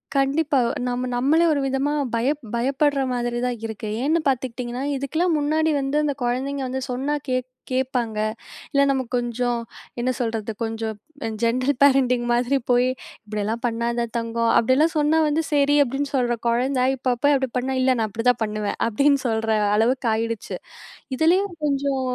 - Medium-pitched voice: No, very high, 255 Hz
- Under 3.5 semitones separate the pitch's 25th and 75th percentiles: Yes, average, 3.0 semitones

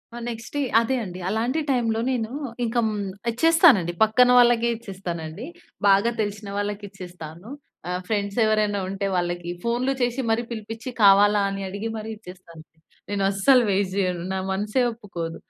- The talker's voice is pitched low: No, high, 205 Hz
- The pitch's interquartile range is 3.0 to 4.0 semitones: Yes, average, 3.3 semitones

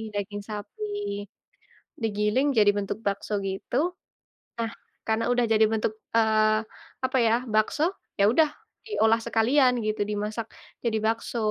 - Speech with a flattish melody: Yes, narrow, 1.7 semitones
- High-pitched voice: Yes, high, 220 Hz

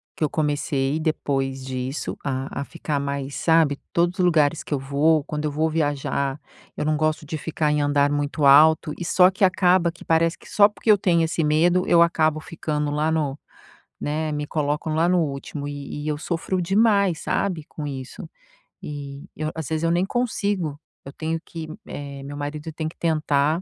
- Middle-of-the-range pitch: Yes, medium, 155 Hz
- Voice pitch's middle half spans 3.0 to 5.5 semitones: No, narrow, 2.4 semitones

